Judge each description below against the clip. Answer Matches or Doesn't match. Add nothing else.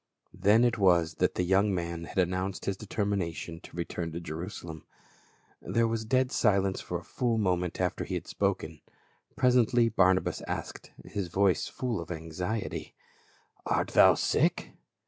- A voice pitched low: Matches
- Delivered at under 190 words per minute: Matches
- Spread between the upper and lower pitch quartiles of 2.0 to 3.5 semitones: Doesn't match